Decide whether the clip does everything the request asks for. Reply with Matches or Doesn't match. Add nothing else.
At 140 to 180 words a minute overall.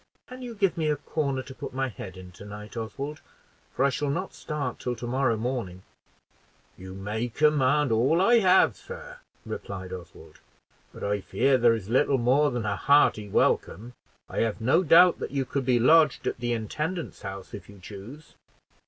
Doesn't match